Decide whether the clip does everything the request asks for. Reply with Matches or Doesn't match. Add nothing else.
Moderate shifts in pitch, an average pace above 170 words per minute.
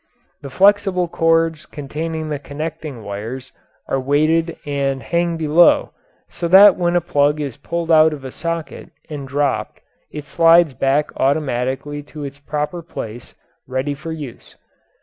Doesn't match